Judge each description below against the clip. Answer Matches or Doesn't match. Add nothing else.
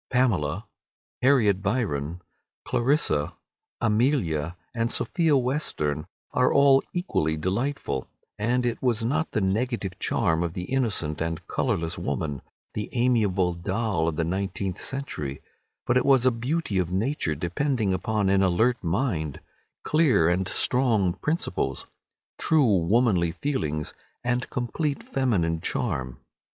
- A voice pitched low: Matches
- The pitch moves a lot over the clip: Matches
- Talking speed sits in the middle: Doesn't match